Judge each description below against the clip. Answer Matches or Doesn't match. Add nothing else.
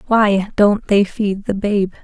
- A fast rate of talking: Doesn't match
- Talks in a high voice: Matches